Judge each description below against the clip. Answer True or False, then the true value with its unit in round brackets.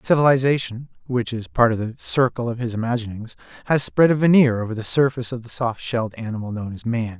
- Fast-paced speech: True (210 wpm)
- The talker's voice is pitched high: False (120 Hz)